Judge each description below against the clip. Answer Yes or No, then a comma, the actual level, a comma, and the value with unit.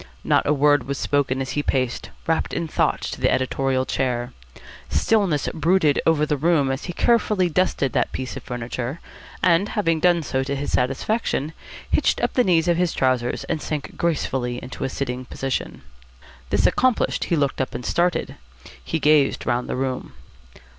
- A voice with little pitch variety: No, average, 4.4 semitones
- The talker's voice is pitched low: No, medium, 145 Hz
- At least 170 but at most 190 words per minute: Yes, average, 175 wpm